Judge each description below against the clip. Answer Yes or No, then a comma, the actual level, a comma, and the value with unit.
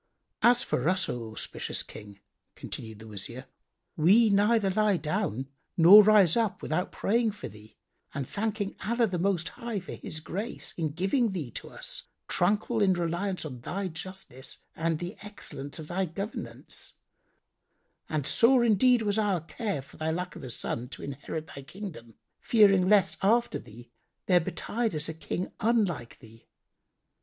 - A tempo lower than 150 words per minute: No, average, 160 wpm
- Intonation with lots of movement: Yes, wide, 5.8 semitones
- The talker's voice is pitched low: No, medium, 185 Hz